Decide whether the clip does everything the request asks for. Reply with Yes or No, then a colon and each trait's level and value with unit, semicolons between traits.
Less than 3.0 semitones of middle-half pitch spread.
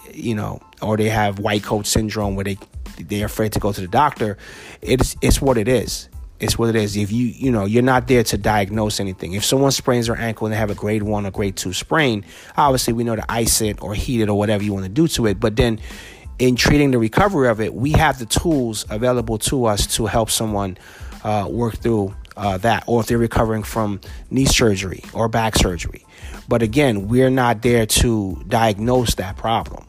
Yes: narrow, 2.6 semitones